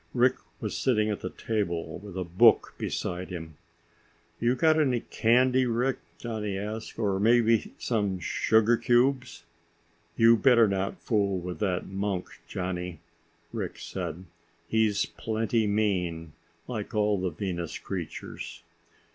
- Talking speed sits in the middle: No, slow, 130 wpm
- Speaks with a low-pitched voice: Yes, low, 105 Hz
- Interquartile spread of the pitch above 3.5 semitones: Yes, average, 4.1 semitones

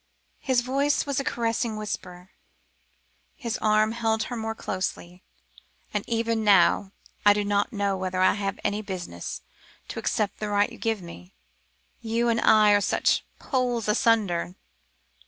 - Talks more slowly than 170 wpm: Yes, average, 150 wpm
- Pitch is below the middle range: No, high, 215 Hz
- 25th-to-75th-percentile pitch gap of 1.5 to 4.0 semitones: Yes, average, 2.7 semitones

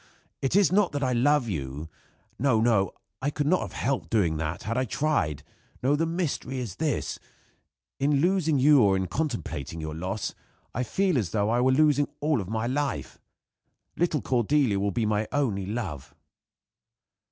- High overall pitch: No, low, 125 Hz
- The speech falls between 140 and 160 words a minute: No, average, 175 wpm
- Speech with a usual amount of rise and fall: No, wide, 6.8 semitones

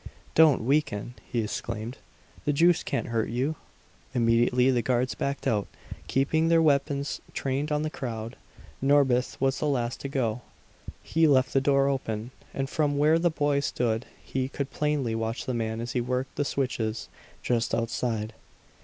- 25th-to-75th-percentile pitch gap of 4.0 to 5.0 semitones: No, average, 3.4 semitones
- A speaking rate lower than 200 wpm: Yes, average, 160 wpm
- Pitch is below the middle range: Yes, low, 130 Hz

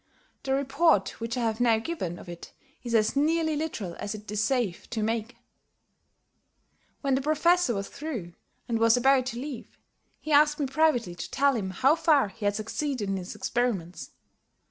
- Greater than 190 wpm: No, average, 185 wpm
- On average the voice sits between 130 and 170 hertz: No, high, 240 Hz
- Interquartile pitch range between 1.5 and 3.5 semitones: No, wide, 5.4 semitones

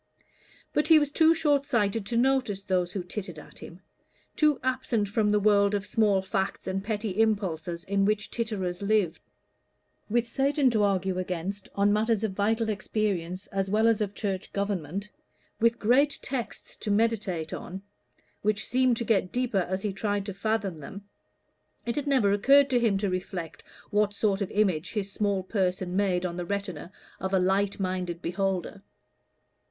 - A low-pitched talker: No, high, 200 Hz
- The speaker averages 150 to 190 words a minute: Yes, average, 170 wpm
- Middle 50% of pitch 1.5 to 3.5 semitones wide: Yes, average, 3.0 semitones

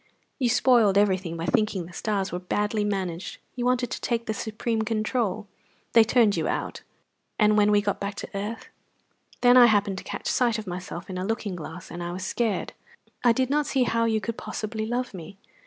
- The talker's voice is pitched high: Yes, high, 210 Hz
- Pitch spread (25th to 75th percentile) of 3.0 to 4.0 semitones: Yes, average, 3.4 semitones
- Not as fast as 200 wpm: No, fast, 205 wpm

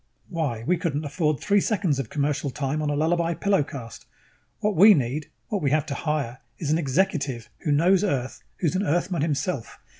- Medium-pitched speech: Yes, medium, 155 Hz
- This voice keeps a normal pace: Yes, average, 190 wpm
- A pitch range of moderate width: Yes, average, 4.0 semitones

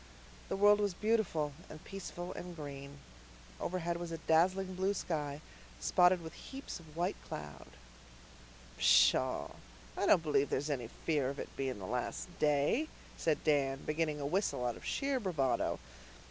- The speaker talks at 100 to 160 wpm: Yes, average, 155 wpm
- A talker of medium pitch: Yes, medium, 160 Hz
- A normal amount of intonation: Yes, average, 4.7 semitones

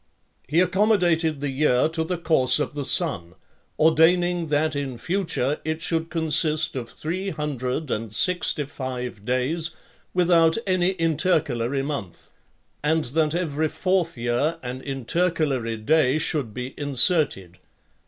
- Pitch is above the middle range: No, medium, 155 Hz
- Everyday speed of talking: No, slow, 130 wpm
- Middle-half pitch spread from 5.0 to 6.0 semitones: No, average, 4.3 semitones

